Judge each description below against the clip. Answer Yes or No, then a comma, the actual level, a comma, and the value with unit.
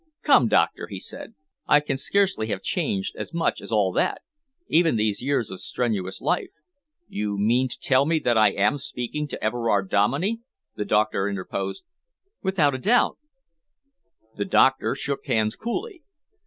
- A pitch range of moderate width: No, wide, 7.9 semitones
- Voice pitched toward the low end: Yes, low, 130 Hz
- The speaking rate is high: No, average, 160 wpm